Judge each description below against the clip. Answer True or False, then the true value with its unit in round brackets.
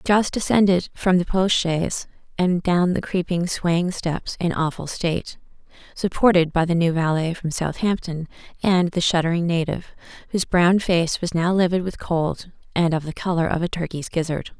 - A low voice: False (175 Hz)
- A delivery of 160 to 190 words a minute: True (175 wpm)